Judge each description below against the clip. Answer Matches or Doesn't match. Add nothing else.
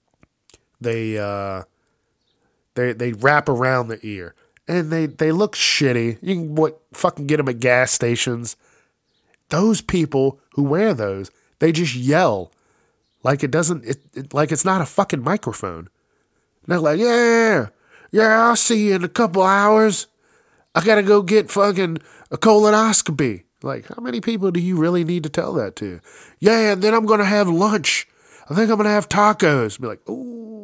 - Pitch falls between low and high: Matches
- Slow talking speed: Doesn't match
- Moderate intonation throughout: Doesn't match